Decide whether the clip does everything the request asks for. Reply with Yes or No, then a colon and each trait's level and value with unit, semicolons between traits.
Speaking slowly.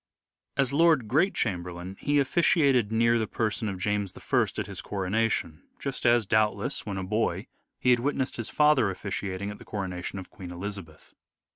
No: average, 170 wpm